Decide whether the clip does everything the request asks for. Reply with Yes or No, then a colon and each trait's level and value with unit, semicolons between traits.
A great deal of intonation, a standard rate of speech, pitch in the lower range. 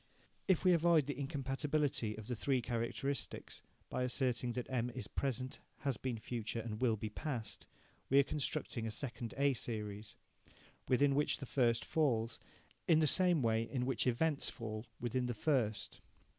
No: average, 3.5 semitones; average, 165 wpm; low, 125 Hz